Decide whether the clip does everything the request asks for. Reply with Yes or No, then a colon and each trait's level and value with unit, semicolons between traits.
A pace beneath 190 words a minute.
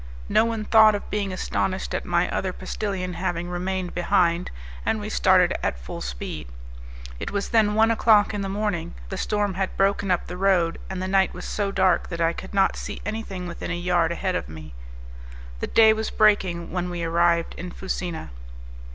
No: average, 195 wpm